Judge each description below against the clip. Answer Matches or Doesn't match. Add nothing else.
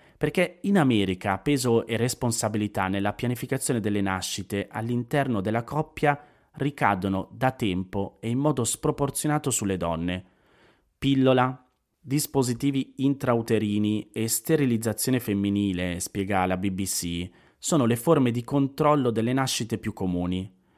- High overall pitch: Doesn't match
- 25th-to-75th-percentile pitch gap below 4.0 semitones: Doesn't match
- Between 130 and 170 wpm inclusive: Doesn't match